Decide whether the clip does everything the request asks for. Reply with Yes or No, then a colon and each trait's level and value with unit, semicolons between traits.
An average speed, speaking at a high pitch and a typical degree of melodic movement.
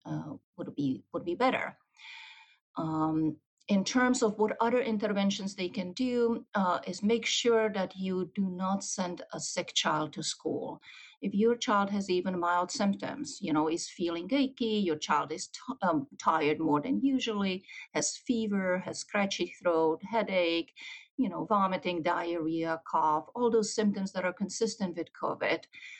Yes: average, 160 wpm; high, 195 Hz; average, 4.7 semitones